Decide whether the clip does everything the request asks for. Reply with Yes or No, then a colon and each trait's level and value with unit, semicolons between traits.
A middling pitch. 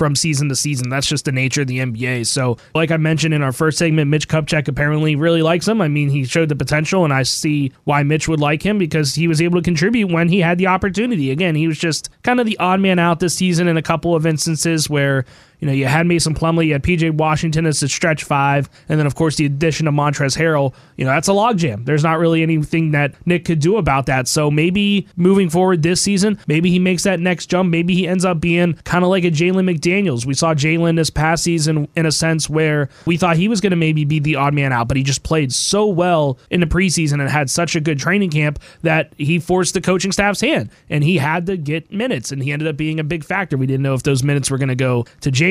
Yes: medium, 160 Hz